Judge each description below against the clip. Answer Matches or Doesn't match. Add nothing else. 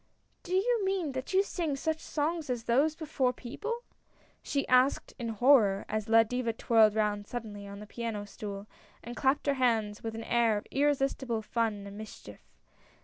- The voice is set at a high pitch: Matches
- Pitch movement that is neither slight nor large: Matches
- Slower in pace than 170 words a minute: Doesn't match